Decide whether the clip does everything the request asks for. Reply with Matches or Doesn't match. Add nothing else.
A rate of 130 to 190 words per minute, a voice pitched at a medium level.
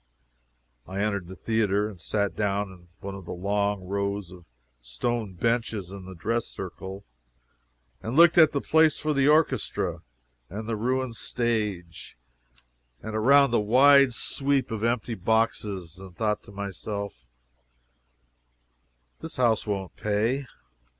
Doesn't match